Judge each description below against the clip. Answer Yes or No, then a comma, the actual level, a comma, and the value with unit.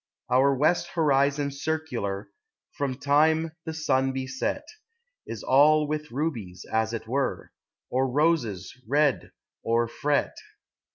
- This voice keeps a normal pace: No, slow, 115 wpm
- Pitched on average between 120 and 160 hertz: Yes, medium, 140 Hz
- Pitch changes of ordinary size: Yes, average, 3.3 semitones